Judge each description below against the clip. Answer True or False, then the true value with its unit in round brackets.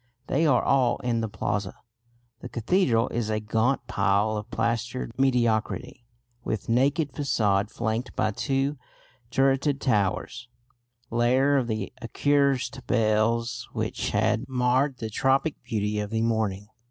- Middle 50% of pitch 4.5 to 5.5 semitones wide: False (3.6 semitones)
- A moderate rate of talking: False (130 wpm)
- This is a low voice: True (120 Hz)